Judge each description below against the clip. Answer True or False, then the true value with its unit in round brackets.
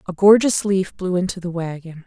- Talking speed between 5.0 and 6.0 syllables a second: True (5.3 syllables/s)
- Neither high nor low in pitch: True (180 Hz)